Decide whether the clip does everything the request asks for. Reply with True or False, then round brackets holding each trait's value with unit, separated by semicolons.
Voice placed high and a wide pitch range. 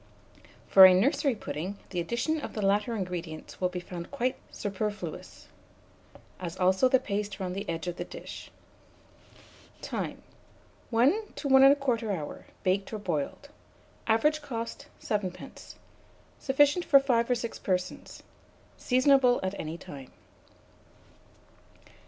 True (210 Hz; 5.9 semitones)